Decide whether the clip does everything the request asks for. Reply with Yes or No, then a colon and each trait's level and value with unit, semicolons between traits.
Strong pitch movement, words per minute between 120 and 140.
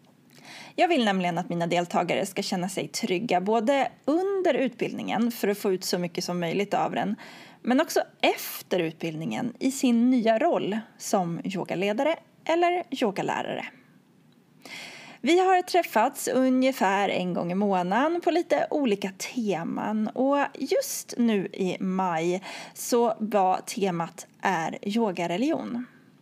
Yes: wide, 5.8 semitones; average, 130 wpm